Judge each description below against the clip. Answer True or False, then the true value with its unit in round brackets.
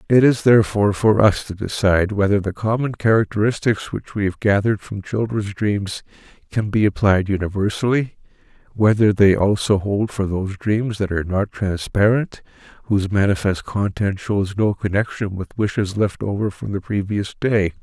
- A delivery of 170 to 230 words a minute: False (160 wpm)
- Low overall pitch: True (100 Hz)